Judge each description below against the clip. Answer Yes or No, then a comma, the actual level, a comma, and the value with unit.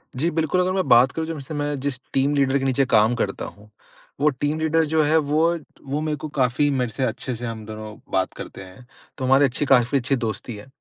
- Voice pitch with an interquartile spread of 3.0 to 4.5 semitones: Yes, average, 3.9 semitones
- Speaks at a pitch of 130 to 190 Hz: Yes, low, 135 Hz